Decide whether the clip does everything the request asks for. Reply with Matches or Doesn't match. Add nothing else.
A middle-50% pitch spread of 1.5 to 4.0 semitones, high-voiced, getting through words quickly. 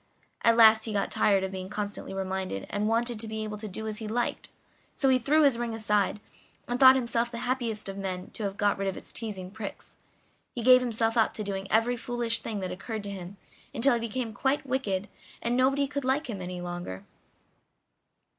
Matches